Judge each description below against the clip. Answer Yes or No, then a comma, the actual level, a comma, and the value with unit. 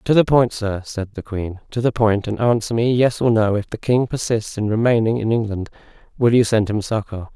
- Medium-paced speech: No, fast, 235 wpm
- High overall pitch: No, low, 110 Hz